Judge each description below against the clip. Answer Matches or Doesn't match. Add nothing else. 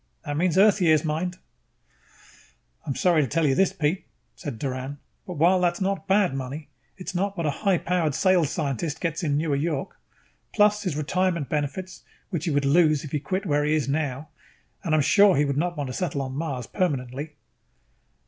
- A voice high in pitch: Doesn't match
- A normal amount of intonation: Matches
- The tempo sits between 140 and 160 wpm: Doesn't match